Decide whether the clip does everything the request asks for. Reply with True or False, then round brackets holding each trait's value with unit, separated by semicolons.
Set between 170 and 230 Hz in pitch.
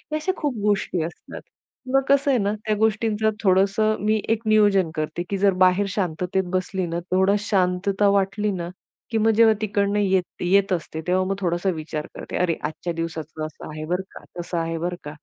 True (190 Hz)